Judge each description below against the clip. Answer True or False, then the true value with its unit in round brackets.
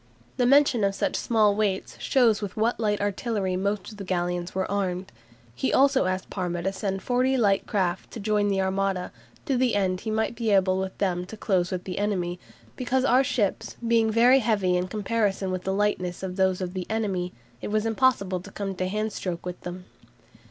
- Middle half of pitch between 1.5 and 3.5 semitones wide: True (3.1 semitones)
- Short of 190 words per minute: False (205 wpm)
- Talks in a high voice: True (200 Hz)